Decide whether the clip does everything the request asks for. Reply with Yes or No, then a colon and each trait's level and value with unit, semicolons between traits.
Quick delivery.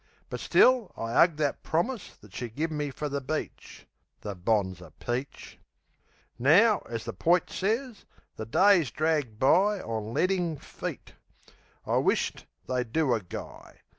No: average, 145 wpm